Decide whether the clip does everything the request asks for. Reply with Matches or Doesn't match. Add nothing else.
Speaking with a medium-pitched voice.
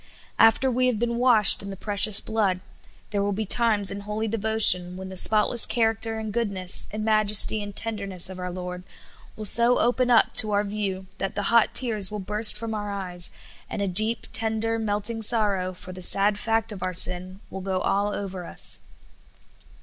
Doesn't match